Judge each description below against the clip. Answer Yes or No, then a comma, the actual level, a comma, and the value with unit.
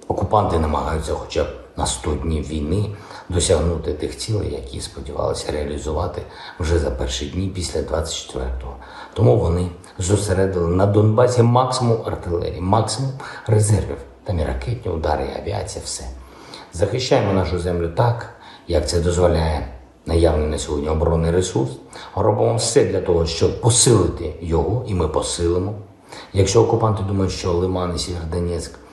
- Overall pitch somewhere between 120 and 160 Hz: No, very low, 90 Hz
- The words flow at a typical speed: Yes, average, 135 wpm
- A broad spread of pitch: No, average, 4.3 semitones